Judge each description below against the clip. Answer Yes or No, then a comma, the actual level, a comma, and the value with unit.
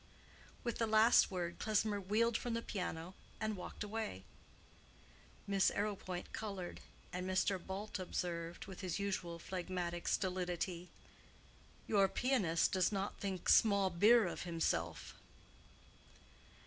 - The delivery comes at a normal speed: No, slow, 120 wpm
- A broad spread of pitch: No, average, 3.0 semitones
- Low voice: No, high, 190 Hz